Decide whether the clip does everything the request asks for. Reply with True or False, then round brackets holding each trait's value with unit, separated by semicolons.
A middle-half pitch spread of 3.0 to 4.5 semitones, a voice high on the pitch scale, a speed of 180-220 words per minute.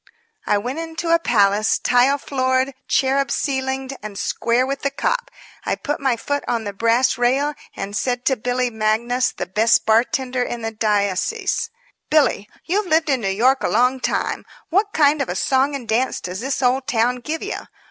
True (3.6 semitones; 255 Hz; 185 wpm)